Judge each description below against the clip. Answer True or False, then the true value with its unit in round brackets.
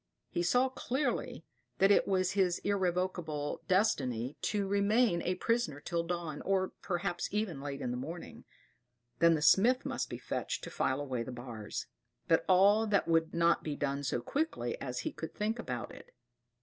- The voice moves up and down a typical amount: False (5.7 semitones)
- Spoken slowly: False (175 wpm)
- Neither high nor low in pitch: True (175 Hz)